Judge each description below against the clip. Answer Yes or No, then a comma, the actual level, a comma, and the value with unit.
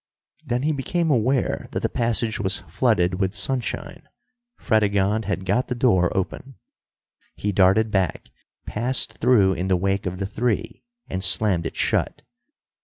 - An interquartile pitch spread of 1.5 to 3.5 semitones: No, average, 4.3 semitones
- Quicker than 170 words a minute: No, average, 150 wpm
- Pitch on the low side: Yes, low, 105 Hz